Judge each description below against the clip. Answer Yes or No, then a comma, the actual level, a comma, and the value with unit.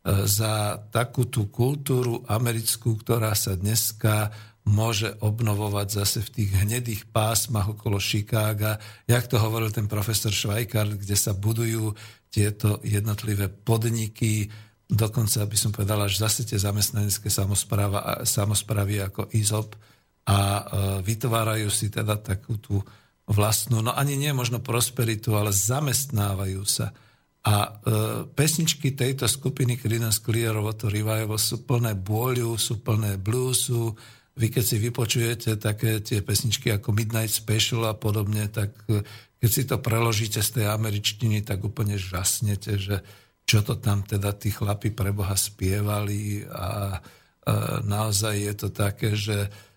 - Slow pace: No, average, 135 wpm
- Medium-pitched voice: No, low, 110 Hz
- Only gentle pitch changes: Yes, narrow, 1.9 semitones